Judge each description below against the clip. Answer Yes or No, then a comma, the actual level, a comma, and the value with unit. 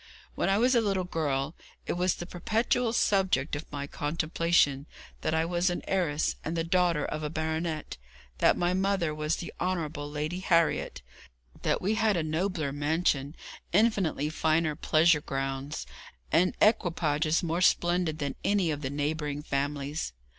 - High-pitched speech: No, medium, 160 Hz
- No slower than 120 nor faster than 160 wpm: Yes, average, 155 wpm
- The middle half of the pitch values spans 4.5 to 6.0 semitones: No, average, 3.4 semitones